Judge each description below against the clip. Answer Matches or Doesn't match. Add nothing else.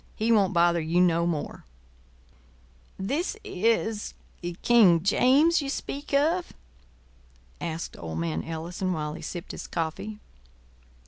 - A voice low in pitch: Doesn't match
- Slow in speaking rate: Matches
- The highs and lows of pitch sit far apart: Matches